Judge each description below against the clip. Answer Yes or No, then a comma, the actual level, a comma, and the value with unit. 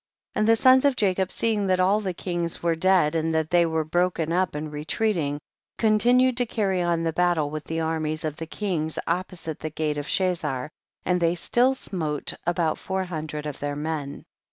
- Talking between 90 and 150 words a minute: No, average, 200 wpm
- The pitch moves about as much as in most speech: Yes, average, 3.4 semitones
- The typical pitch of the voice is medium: Yes, medium, 170 Hz